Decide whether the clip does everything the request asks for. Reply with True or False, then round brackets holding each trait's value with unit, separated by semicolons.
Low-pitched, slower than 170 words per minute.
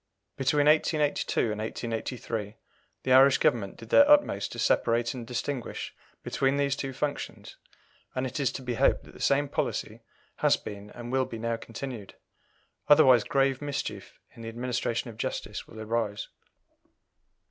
True (125 Hz; 155 wpm)